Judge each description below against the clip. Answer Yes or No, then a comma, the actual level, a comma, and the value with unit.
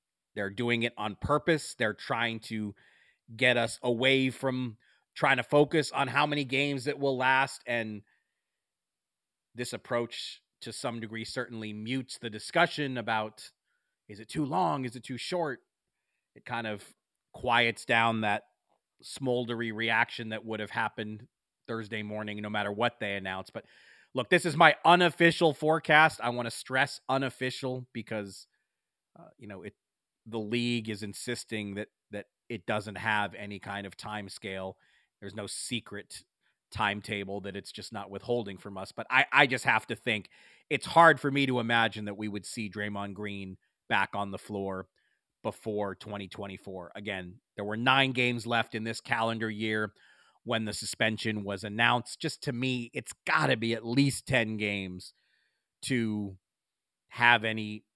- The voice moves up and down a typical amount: Yes, average, 3.6 semitones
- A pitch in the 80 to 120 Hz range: Yes, low, 115 Hz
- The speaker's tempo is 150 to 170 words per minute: Yes, average, 160 wpm